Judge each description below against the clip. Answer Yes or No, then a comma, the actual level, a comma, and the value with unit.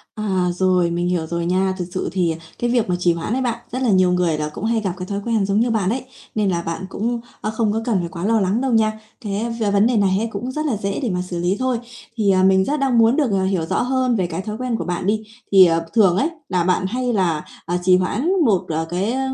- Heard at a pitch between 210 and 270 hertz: No, high, 200 Hz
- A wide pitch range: No, average, 4.1 semitones